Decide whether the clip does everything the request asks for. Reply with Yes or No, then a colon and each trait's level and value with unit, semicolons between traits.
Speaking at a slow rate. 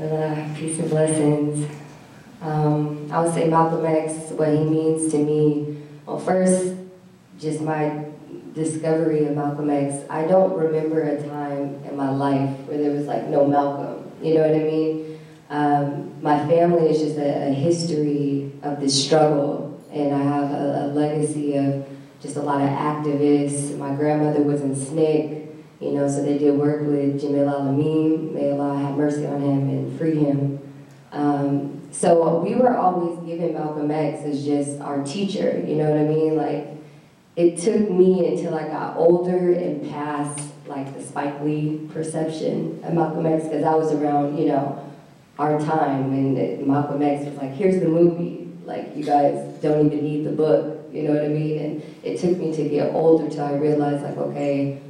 No: average, 180 wpm